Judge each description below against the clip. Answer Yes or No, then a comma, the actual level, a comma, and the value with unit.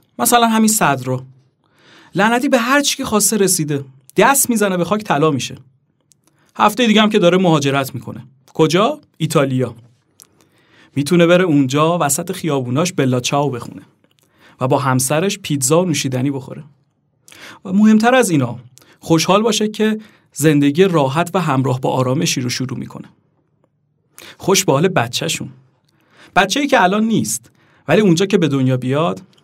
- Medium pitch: Yes, medium, 155 Hz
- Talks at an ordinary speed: Yes, average, 145 wpm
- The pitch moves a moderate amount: No, wide, 5.8 semitones